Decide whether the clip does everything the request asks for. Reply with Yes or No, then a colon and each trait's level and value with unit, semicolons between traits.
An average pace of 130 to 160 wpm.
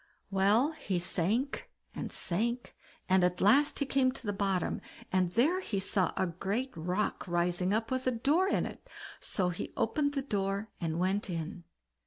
No: average, 175 wpm